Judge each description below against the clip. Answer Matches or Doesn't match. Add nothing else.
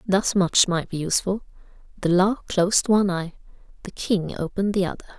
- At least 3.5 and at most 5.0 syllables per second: Doesn't match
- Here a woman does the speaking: Matches